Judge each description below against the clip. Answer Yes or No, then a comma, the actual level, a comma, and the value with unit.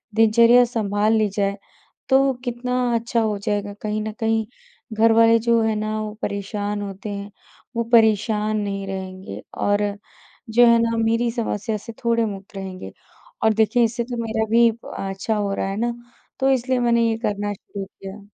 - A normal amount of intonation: No, narrow, 2.2 semitones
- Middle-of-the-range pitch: No, high, 220 Hz